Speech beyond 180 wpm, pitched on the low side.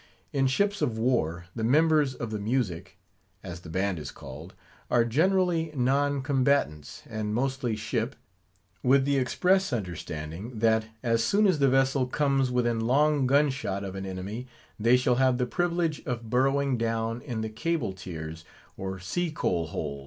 No: average, 165 wpm; low, 120 Hz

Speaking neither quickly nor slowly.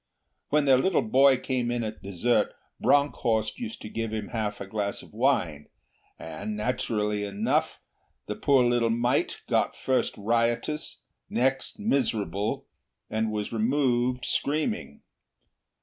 No: slow, 130 wpm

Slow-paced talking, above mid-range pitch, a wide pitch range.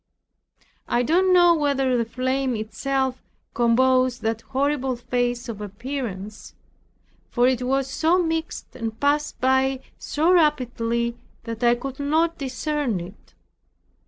No: slow, 125 wpm; very high, 260 Hz; average, 3.3 semitones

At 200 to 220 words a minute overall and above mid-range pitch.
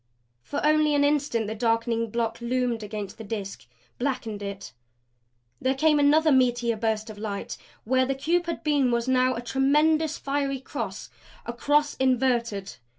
No: average, 155 wpm; very high, 255 Hz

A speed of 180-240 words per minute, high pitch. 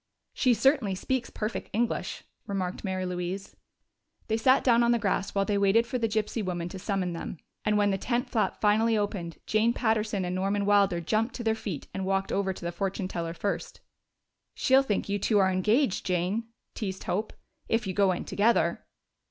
Yes: average, 195 wpm; high, 205 Hz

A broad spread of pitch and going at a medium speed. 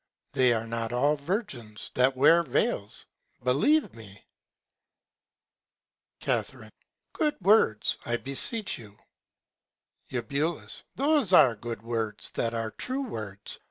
No: wide, 7.4 semitones; slow, 110 wpm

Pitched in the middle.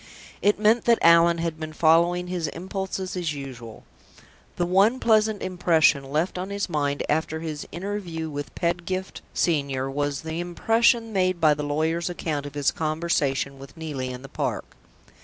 Yes: medium, 165 Hz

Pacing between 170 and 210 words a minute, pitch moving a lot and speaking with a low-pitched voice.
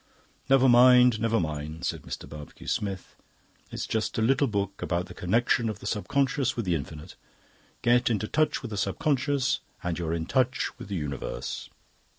Yes: average, 175 wpm; wide, 6.2 semitones; low, 110 Hz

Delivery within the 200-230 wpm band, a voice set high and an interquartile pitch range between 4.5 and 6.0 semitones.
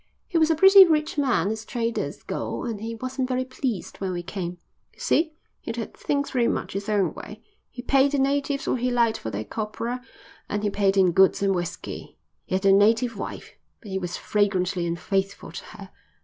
Yes: fast, 205 wpm; high, 220 Hz; average, 5.1 semitones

